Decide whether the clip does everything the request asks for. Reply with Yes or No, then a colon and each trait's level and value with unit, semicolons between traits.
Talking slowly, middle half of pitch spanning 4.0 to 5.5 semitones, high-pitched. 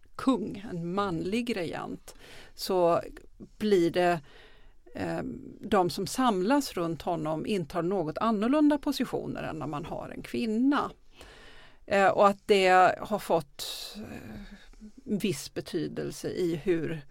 Yes: slow, 120 wpm; average, 4.8 semitones; high, 200 Hz